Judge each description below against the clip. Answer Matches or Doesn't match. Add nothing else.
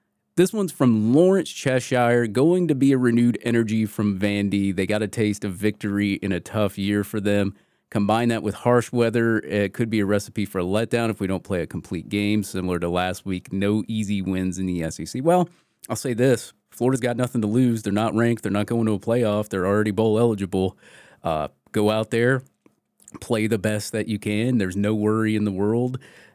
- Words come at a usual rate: Doesn't match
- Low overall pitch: Matches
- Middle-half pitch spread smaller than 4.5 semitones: Matches